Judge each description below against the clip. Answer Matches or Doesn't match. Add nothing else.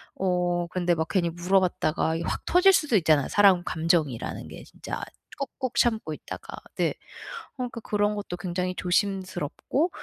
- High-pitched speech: Doesn't match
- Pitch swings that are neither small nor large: Matches